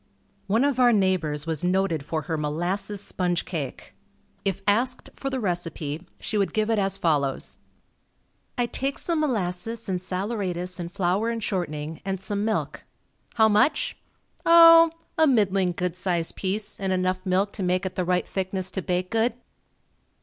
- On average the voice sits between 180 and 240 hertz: Yes, high, 190 Hz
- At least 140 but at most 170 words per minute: Yes, average, 165 wpm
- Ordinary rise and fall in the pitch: Yes, average, 3.5 semitones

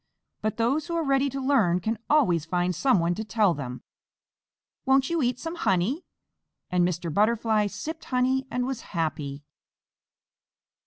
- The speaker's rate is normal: Yes, average, 150 wpm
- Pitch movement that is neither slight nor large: No, wide, 7.3 semitones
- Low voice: No, high, 225 Hz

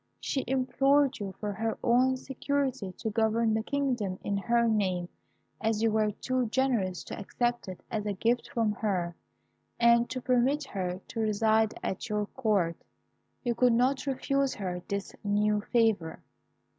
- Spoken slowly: No, average, 155 wpm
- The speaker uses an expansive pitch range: No, average, 3.7 semitones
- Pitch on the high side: Yes, high, 225 Hz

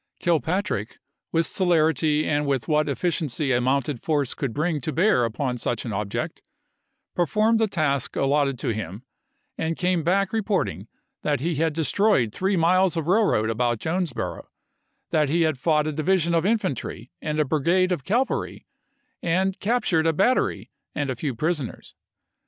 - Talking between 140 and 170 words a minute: Yes, average, 165 wpm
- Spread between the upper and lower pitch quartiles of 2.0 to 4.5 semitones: No, average, 4.9 semitones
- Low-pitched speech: No, medium, 155 Hz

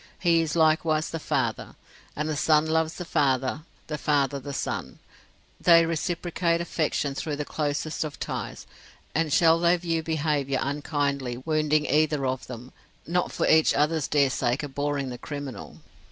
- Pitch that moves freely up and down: No, narrow, 2.4 semitones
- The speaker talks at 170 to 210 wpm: No, average, 155 wpm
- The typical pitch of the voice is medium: Yes, medium, 150 Hz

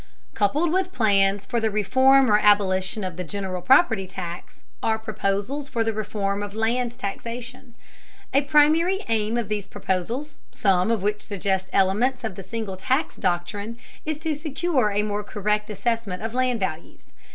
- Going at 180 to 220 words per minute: No, average, 165 wpm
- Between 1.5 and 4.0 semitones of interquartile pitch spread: No, average, 4.4 semitones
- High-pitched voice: Yes, high, 215 Hz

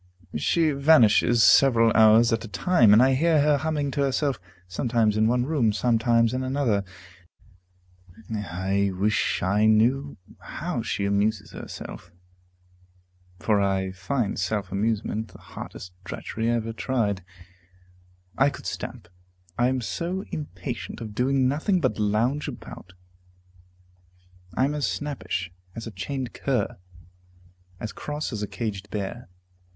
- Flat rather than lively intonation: No, average, 4.8 semitones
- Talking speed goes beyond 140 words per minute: No, slow, 135 wpm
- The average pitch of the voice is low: Yes, low, 115 Hz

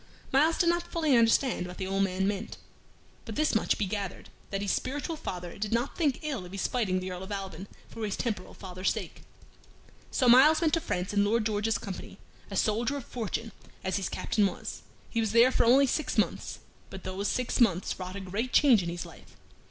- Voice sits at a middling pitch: No, high, 210 Hz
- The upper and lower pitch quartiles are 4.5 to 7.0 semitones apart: Yes, average, 5.0 semitones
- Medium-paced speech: No, fast, 215 wpm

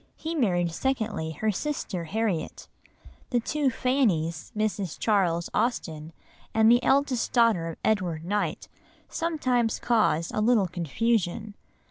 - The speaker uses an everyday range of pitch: No, wide, 6.0 semitones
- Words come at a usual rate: No, slow, 120 wpm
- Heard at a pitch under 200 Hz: No, high, 215 Hz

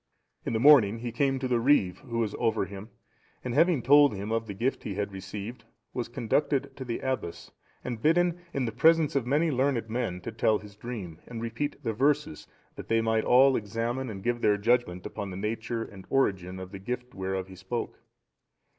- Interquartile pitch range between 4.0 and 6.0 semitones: Yes, average, 4.3 semitones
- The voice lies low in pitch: Yes, low, 115 Hz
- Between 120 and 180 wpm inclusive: No, fast, 205 wpm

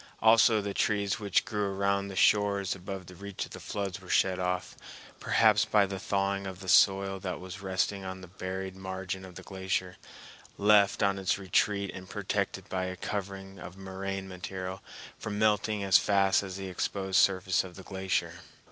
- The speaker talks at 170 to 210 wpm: Yes, average, 175 wpm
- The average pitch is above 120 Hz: No, very low, 95 Hz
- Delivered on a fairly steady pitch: Yes, narrow, 1.1 semitones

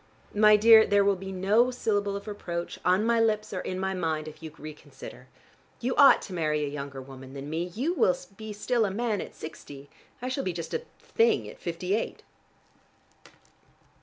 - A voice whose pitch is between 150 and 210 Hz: Yes, high, 190 Hz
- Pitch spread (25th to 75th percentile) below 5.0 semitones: No, average, 5.3 semitones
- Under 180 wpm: No, average, 195 wpm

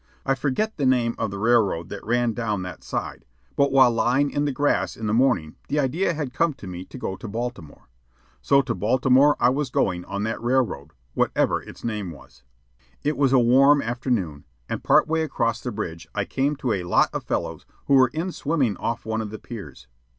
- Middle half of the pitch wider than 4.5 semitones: Yes, average, 5.2 semitones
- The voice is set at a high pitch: No, low, 120 Hz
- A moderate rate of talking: No, fast, 210 wpm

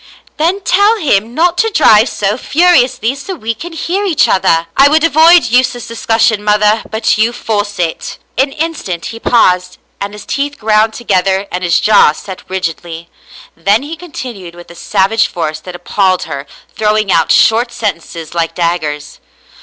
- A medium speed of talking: Yes, average, 175 wpm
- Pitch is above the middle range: Yes, high, 215 Hz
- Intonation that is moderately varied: No, wide, 7.1 semitones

